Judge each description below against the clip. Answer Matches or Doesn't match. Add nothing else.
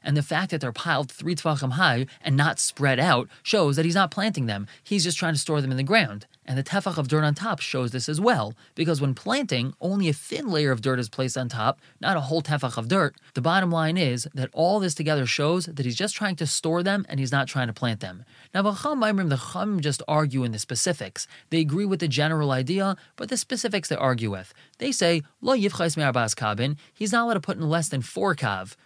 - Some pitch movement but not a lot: Doesn't match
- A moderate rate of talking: Doesn't match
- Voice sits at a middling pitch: Matches